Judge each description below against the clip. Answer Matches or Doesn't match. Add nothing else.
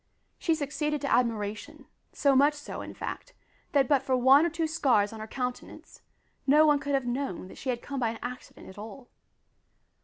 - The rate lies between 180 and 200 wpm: Matches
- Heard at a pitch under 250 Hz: Doesn't match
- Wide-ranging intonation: Doesn't match